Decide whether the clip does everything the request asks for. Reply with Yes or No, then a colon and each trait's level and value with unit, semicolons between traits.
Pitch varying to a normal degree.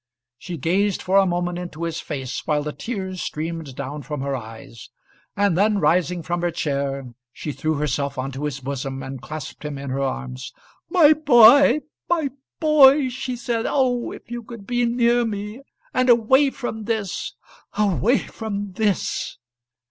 No: wide, 8.8 semitones